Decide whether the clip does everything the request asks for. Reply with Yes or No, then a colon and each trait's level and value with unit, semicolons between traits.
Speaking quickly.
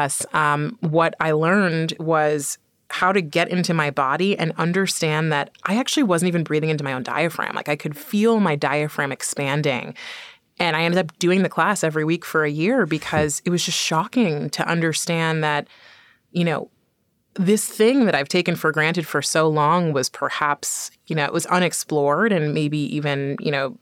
No: average, 185 wpm